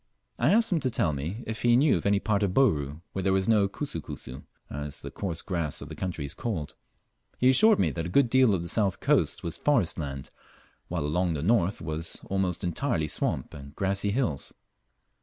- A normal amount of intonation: No, wide, 6.6 semitones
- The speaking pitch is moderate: No, very low, 95 Hz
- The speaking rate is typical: No, fast, 215 wpm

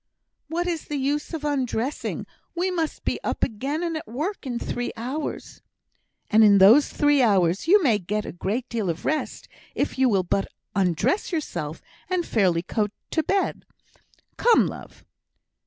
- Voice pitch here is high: Yes, very high, 260 Hz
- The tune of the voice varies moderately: No, wide, 7.3 semitones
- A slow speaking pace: No, average, 165 wpm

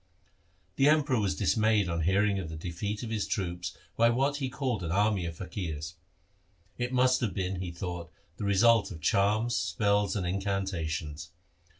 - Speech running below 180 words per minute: Yes, average, 170 wpm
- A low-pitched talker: Yes, low, 100 Hz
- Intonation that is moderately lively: Yes, average, 4.4 semitones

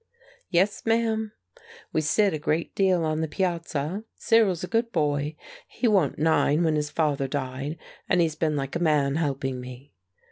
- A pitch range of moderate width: Yes, average, 4.4 semitones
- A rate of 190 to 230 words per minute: No, average, 170 wpm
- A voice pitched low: No, medium, 160 Hz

